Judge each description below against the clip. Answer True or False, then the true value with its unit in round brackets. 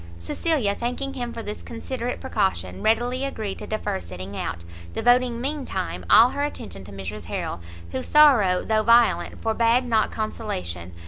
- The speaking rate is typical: True (155 wpm)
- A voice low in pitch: False (225 Hz)